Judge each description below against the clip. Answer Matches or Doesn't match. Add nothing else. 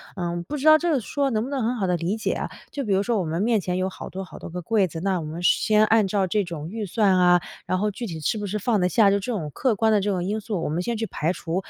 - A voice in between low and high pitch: Doesn't match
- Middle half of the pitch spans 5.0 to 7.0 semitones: Doesn't match